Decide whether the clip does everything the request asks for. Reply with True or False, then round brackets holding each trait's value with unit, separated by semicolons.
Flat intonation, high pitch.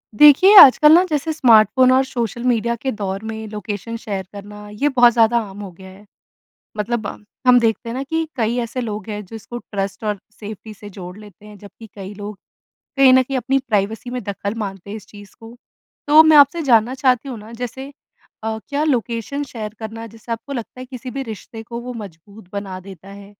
False (3.7 semitones; 225 Hz)